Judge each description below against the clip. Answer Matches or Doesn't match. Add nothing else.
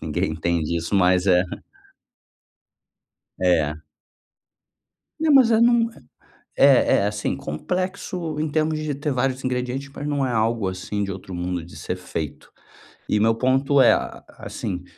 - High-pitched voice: Doesn't match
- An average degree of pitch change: Doesn't match